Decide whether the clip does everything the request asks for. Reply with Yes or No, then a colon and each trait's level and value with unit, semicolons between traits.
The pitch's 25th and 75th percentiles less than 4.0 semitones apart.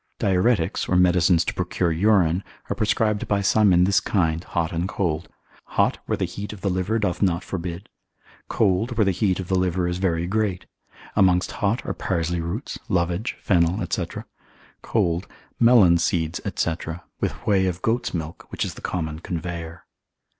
Yes: average, 2.8 semitones